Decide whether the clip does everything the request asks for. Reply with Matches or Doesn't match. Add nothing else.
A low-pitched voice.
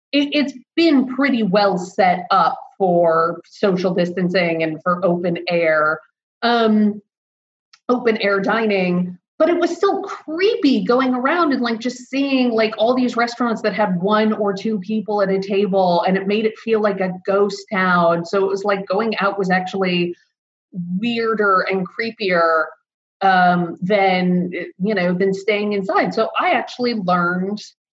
Doesn't match